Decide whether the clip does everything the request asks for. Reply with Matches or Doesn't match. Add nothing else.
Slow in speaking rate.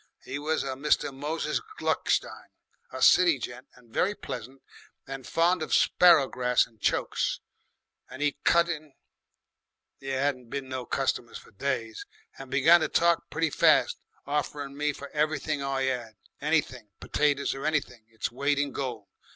Doesn't match